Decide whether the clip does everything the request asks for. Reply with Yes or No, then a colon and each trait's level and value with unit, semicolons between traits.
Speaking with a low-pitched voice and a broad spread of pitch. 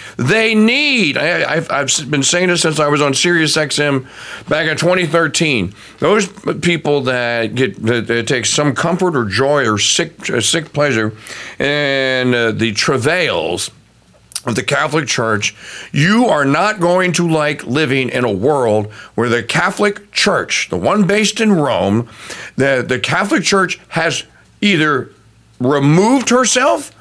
No: medium, 150 Hz; wide, 6.9 semitones